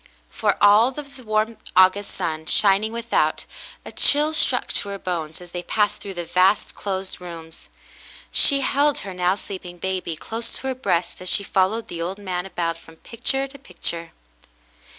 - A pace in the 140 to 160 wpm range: No, average, 175 wpm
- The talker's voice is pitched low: No, high, 195 Hz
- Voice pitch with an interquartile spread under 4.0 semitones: No, average, 4.3 semitones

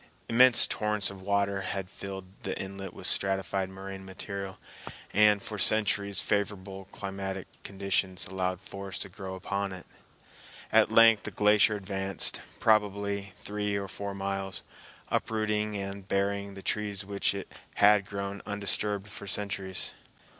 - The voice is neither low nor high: No, low, 100 Hz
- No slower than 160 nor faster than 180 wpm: No, slow, 135 wpm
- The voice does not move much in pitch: Yes, narrow, 1.1 semitones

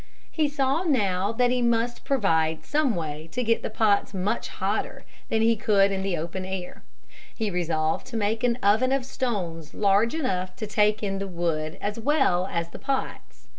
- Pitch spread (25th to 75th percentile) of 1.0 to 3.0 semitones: No, average, 4.9 semitones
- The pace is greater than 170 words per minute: Yes, average, 180 wpm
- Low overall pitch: No, high, 205 Hz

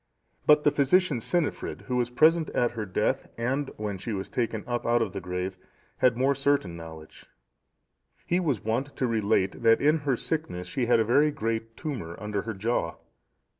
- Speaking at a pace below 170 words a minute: No, average, 185 wpm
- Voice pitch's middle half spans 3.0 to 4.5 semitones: No, wide, 5.4 semitones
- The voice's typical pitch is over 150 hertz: No, low, 120 Hz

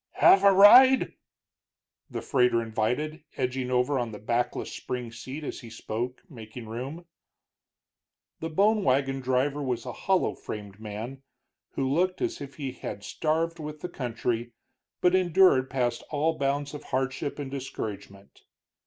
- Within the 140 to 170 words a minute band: Yes, average, 145 wpm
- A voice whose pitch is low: Yes, low, 130 Hz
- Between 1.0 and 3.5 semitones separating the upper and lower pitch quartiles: No, average, 4.5 semitones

